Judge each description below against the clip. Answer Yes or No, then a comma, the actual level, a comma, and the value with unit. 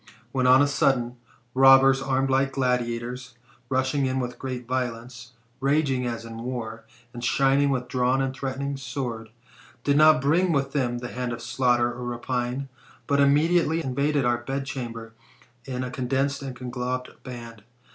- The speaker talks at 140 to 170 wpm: Yes, average, 155 wpm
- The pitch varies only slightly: Yes, narrow, 1.9 semitones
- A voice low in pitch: Yes, low, 130 Hz